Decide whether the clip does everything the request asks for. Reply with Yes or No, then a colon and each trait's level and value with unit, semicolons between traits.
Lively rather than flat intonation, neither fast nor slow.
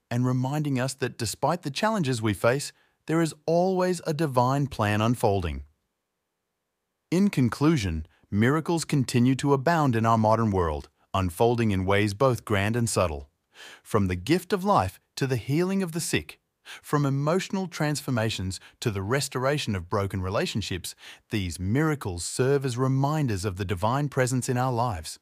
Yes: wide, 6.0 semitones; average, 155 wpm